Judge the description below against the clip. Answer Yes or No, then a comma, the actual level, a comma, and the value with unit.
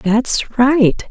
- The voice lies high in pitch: Yes, high, 245 Hz